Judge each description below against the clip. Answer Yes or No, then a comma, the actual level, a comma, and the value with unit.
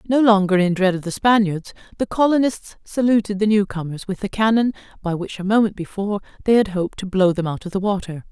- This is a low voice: No, high, 200 Hz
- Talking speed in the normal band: No, fast, 225 wpm